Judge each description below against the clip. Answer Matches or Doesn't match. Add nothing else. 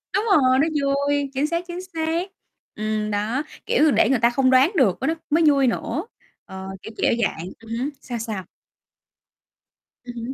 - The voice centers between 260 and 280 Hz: Matches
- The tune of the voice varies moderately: Matches